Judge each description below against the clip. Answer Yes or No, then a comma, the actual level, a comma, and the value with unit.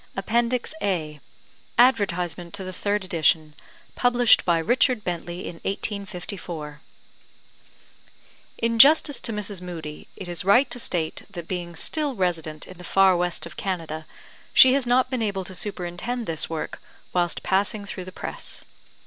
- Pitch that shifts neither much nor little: Yes, average, 4.7 semitones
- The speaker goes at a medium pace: Yes, average, 150 wpm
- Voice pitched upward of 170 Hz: Yes, medium, 185 Hz